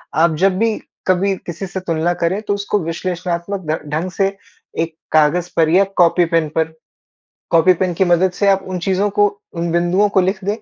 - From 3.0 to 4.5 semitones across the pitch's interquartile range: No, narrow, 2.6 semitones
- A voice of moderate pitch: Yes, medium, 180 Hz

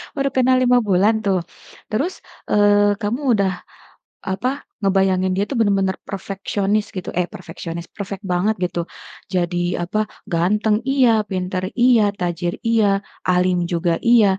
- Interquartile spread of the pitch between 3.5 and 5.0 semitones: No, average, 2.9 semitones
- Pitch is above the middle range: Yes, high, 195 Hz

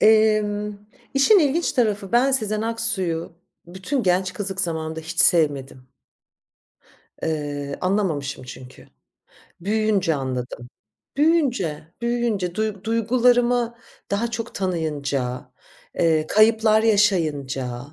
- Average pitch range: No, wide, 6.4 semitones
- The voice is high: Yes, high, 195 Hz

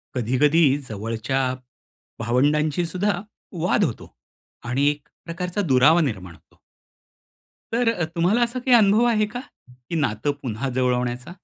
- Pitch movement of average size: No, wide, 6.6 semitones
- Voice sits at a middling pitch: Yes, medium, 150 Hz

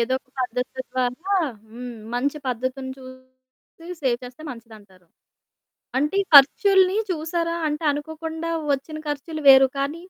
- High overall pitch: Yes, very high, 270 Hz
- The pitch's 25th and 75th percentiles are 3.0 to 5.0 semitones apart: Yes, average, 4.1 semitones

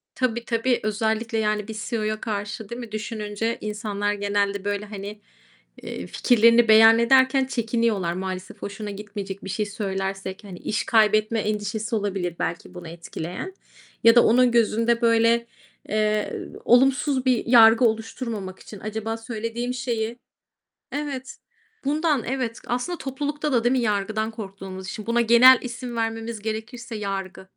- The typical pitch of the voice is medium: No, high, 220 Hz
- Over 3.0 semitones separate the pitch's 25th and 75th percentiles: No, narrow, 2.5 semitones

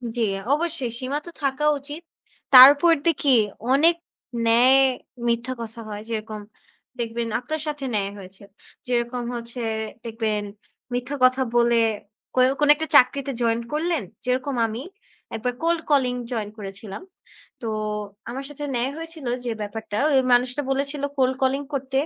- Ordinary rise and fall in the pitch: Yes, average, 3.5 semitones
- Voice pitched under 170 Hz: No, very high, 255 Hz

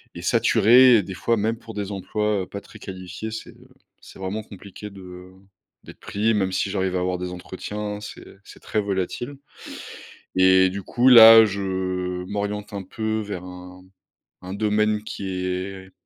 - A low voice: Yes, low, 100 Hz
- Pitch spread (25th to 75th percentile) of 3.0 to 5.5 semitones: No, narrow, 2.5 semitones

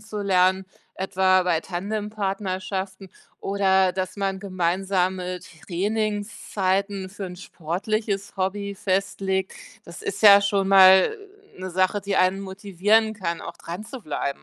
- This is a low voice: No, high, 190 Hz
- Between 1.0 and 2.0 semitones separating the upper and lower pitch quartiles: Yes, narrow, 1.4 semitones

